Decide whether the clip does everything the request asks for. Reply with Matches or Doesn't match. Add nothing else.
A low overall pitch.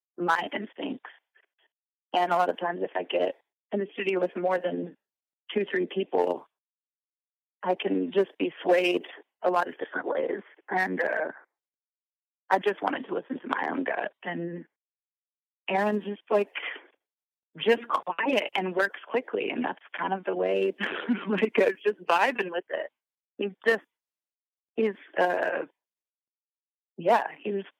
Doesn't match